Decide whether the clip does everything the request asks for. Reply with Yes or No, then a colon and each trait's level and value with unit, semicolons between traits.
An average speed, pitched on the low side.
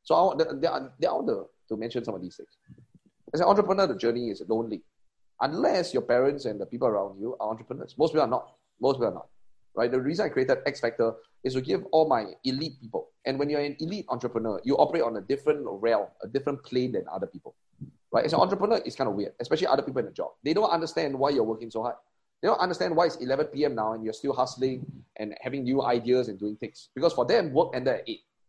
No: fast, 245 wpm; low, 130 Hz